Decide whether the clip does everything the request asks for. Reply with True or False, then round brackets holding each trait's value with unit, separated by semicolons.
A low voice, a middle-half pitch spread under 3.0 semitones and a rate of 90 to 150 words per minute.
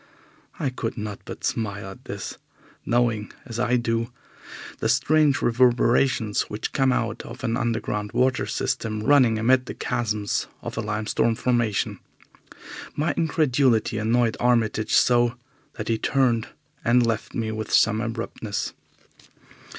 True (115 Hz; 2.4 semitones; 135 wpm)